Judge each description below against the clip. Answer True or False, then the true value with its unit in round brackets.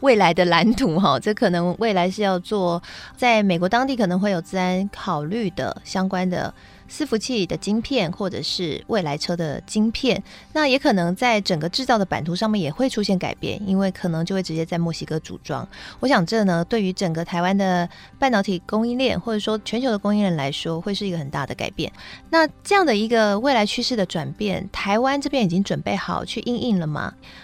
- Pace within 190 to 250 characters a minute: False (315 characters per minute)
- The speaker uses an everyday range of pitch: True (4.3 semitones)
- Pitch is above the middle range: True (195 Hz)